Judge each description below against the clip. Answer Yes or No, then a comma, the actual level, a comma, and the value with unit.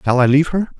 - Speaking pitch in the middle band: Yes, medium, 145 Hz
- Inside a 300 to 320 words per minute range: Yes, fast, 305 wpm